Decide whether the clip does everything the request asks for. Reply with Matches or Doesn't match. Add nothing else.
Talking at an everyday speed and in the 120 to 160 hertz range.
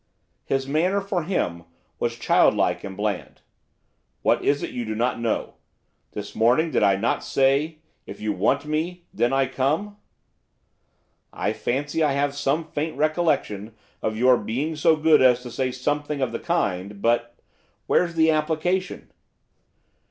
Matches